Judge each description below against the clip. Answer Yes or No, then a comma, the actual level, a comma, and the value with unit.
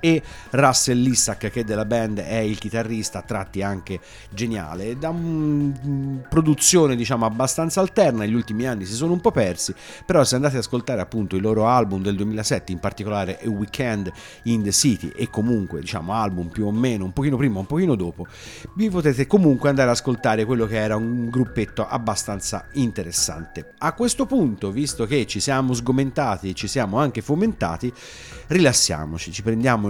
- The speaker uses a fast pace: Yes, fast, 175 wpm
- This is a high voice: No, low, 115 Hz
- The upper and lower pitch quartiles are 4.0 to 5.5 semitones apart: Yes, average, 4.8 semitones